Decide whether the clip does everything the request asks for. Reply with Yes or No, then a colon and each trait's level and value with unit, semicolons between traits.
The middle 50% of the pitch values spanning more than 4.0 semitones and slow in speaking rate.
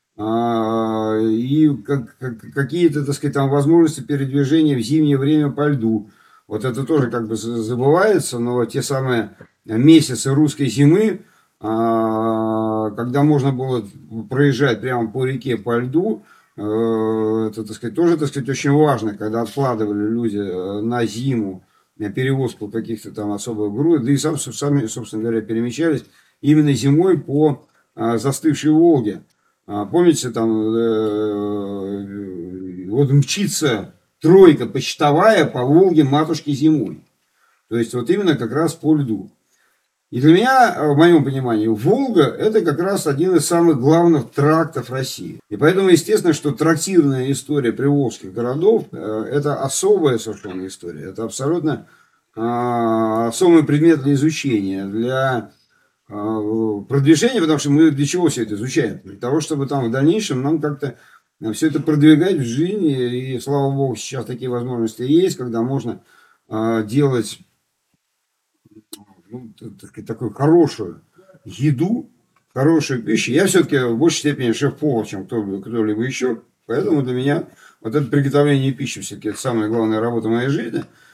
No: average, 5.1 semitones; average, 135 wpm